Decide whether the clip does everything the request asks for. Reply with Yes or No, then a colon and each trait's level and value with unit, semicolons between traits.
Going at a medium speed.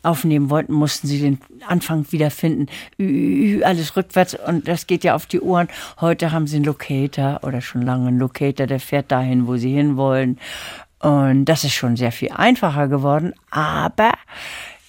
Yes: average, 170 wpm